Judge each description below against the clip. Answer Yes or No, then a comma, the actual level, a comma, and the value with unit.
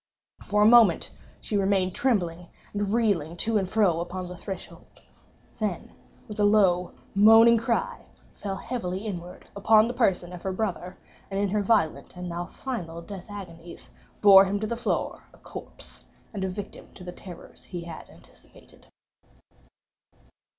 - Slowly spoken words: No, average, 155 wpm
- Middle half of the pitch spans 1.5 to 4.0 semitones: Yes, average, 3.2 semitones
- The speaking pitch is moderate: No, high, 195 Hz